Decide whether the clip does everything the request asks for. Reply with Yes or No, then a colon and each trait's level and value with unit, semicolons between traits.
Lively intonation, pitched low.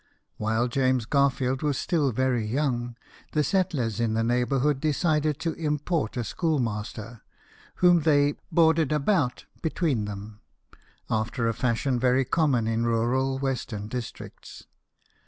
No: average, 4.4 semitones; low, 130 Hz